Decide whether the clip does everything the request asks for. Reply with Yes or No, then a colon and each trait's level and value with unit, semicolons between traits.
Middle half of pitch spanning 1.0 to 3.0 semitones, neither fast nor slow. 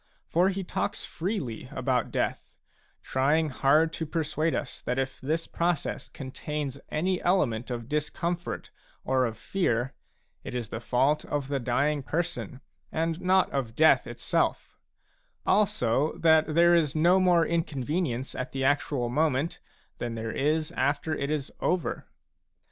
No: average, 4.1 semitones; average, 145 wpm